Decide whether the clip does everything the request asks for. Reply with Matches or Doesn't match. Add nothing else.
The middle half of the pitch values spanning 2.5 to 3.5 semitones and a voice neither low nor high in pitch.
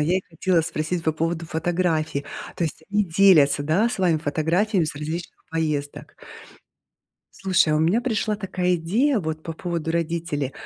Matches